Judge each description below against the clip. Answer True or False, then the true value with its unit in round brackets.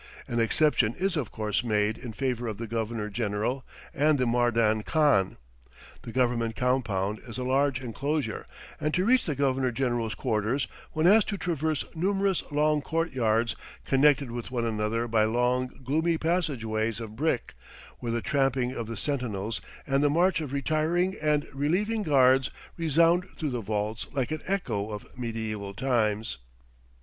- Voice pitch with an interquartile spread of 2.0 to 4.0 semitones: False (5.2 semitones)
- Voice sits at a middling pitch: False (125 Hz)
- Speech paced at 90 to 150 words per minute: False (160 wpm)